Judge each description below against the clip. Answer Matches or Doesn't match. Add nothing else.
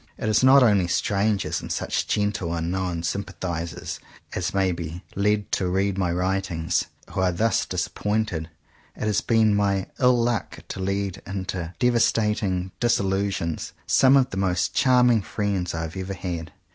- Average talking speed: Matches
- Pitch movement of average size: Matches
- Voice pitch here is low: Matches